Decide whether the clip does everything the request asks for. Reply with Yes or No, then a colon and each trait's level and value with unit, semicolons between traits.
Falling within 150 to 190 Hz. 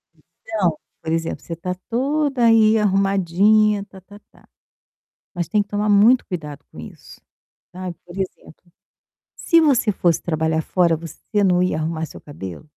Yes: medium, 185 Hz